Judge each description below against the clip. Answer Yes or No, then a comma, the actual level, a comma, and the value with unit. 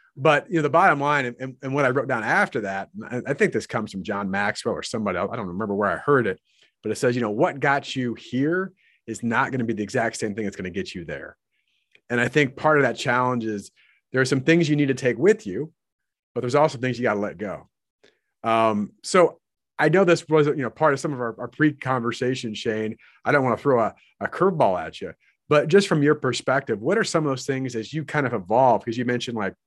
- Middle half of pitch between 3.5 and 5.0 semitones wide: Yes, average, 4.1 semitones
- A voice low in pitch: Yes, low, 130 Hz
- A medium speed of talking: No, fast, 260 wpm